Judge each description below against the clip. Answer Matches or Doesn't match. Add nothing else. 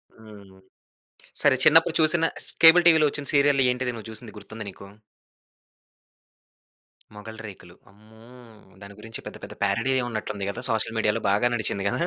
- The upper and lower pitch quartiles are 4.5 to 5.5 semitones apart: Matches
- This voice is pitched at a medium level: Doesn't match